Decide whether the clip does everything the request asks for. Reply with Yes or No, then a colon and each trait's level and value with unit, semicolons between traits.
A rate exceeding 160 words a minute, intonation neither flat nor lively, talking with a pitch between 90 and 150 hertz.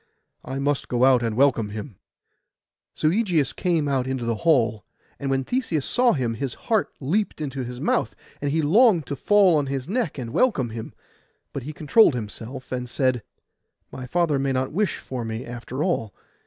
Yes: average, 185 wpm; average, 4.7 semitones; low, 135 Hz